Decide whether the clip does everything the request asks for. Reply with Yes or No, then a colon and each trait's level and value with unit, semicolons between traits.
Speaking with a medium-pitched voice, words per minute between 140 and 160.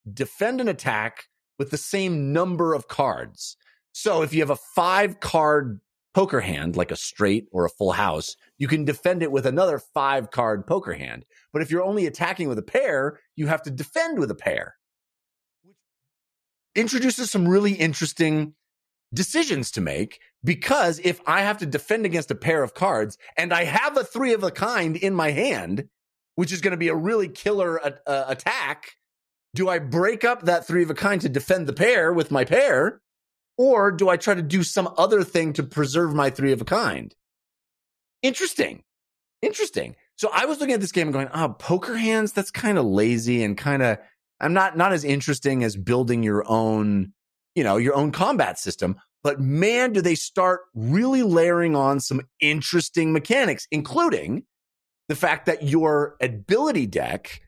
No: medium, 170 Hz; average, 185 wpm